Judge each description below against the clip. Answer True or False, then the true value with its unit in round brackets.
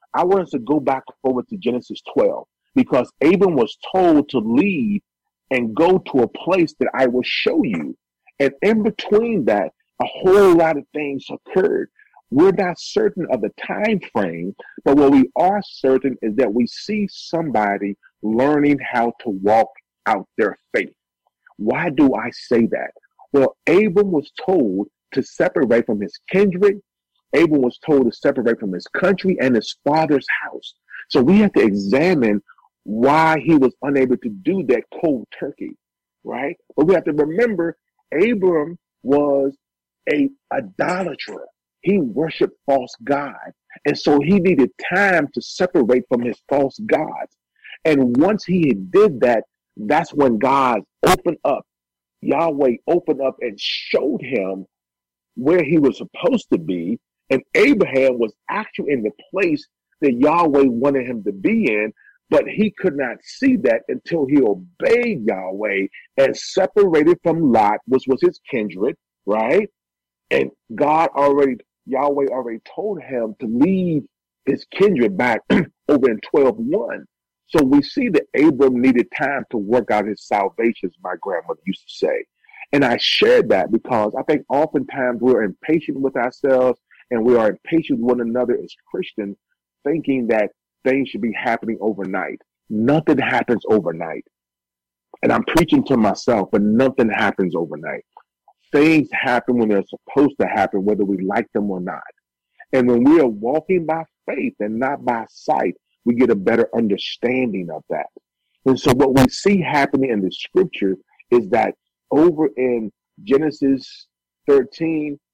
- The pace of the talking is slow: False (155 wpm)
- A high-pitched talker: False (140 Hz)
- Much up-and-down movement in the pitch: True (8.7 semitones)